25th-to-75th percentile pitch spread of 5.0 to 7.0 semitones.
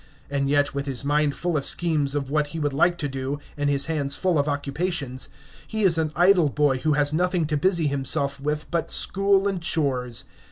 No: average, 3.2 semitones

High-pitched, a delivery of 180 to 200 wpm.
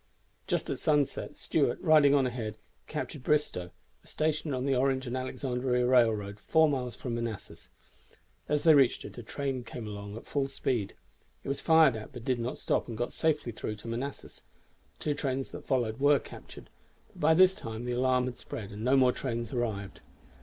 No: low, 125 Hz; average, 190 wpm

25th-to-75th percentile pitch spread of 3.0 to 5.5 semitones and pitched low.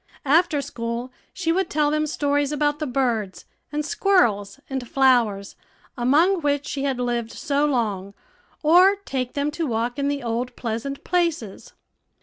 No: average, 4.1 semitones; very high, 275 Hz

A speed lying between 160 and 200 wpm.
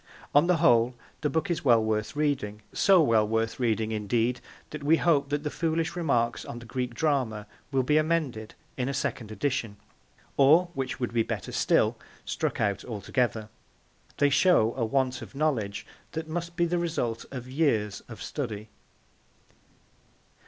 Yes: average, 165 wpm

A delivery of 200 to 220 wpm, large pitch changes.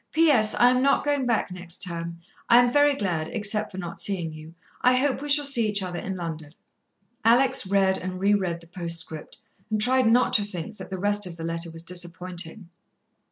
Yes: fast, 205 wpm; wide, 5.9 semitones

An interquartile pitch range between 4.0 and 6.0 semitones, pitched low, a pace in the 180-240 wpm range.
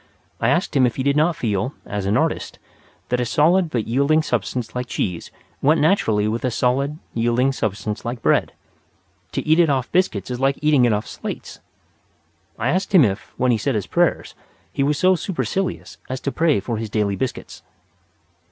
Yes: average, 5.1 semitones; low, 125 Hz; average, 190 wpm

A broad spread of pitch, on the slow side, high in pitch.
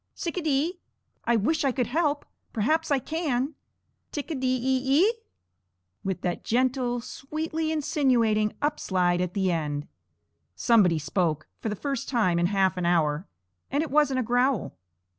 No: wide, 7.4 semitones; average, 160 wpm; very high, 250 Hz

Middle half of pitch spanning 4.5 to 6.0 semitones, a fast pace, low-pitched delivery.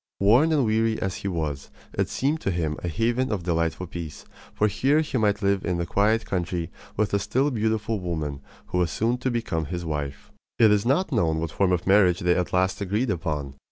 Yes: average, 4.9 semitones; fast, 215 wpm; low, 100 Hz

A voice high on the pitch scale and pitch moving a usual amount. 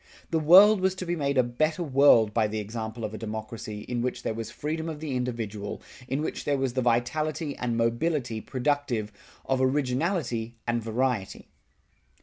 No: low, 125 Hz; average, 4.8 semitones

